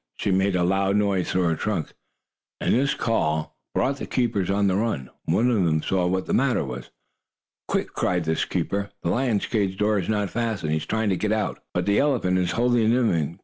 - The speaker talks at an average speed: No, fast, 220 wpm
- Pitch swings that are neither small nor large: Yes, average, 4.0 semitones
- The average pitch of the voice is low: Yes, low, 100 Hz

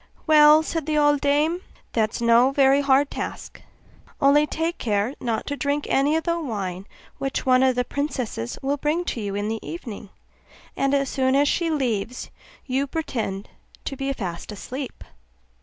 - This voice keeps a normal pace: Yes, average, 175 wpm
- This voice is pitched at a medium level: No, very high, 275 Hz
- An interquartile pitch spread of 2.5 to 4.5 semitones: Yes, average, 4.1 semitones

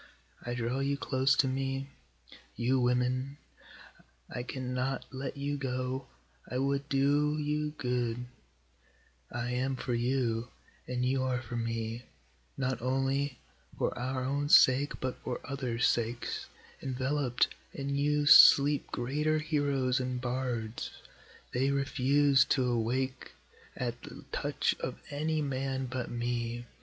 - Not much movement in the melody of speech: Yes, narrow, 2.0 semitones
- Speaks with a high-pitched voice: No, low, 130 Hz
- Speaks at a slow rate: Yes, slow, 130 wpm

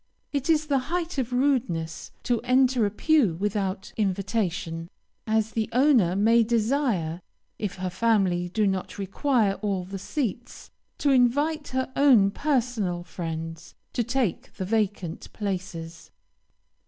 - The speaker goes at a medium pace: No, slow, 130 wpm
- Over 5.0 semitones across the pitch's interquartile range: Yes, wide, 5.6 semitones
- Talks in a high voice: Yes, high, 215 Hz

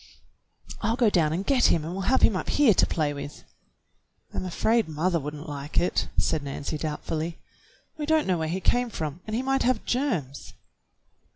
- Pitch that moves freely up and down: Yes, wide, 7.4 semitones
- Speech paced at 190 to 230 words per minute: Yes, average, 195 wpm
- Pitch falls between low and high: Yes, medium, 175 Hz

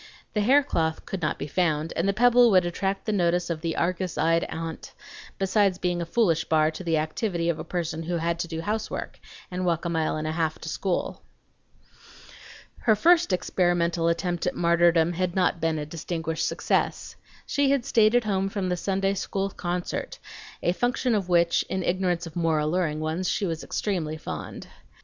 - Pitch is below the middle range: No, medium, 175 Hz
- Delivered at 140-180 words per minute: No, average, 190 wpm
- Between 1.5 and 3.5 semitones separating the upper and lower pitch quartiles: Yes, average, 2.8 semitones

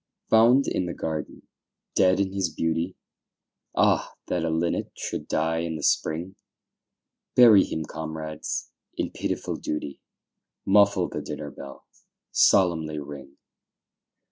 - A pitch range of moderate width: Yes, average, 3.4 semitones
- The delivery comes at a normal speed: No, slow, 120 wpm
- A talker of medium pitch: No, very low, 80 Hz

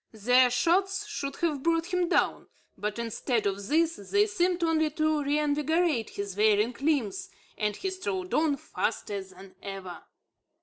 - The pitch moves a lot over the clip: Yes, wide, 8.0 semitones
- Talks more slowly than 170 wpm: Yes, average, 145 wpm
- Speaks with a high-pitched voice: Yes, very high, 285 Hz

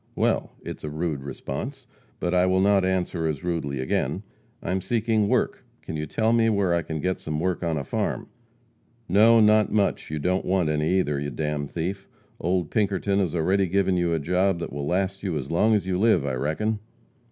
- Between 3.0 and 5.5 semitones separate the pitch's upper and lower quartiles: Yes, average, 4.2 semitones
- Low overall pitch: Yes, very low, 90 Hz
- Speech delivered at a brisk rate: Yes, fast, 210 wpm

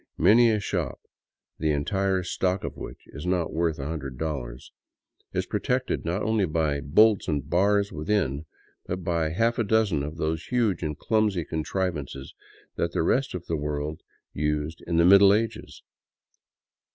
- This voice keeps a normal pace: Yes, average, 165 wpm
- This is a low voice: Yes, very low, 85 Hz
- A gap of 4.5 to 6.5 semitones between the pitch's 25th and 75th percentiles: Yes, average, 5.0 semitones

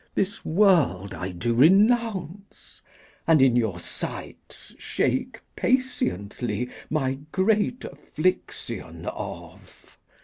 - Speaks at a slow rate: Yes, slow, 90 wpm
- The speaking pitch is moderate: Yes, medium, 155 Hz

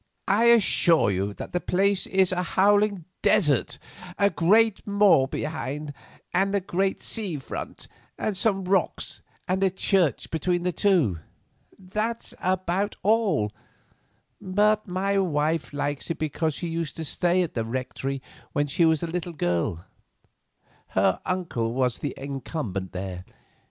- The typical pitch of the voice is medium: Yes, medium, 175 Hz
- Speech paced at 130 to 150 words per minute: Yes, average, 145 wpm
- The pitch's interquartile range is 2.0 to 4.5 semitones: No, wide, 5.4 semitones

